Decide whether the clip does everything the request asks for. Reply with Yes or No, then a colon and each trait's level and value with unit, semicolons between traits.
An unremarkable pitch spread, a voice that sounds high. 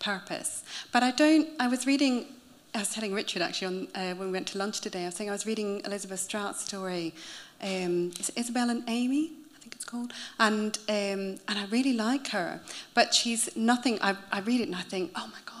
Yes: average, 4.0 semitones; high, 220 Hz